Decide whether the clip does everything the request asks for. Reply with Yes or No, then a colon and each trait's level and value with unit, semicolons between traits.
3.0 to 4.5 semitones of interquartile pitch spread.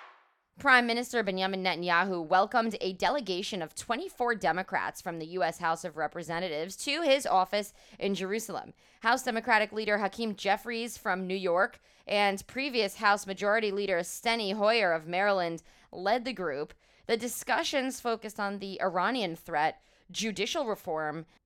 Yes: average, 4.0 semitones